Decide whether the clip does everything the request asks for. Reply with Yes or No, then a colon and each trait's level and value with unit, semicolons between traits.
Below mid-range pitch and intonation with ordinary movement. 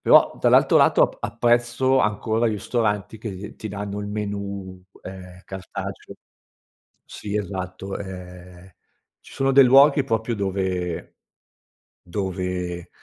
Yes: low, 100 Hz; average, 3.3 semitones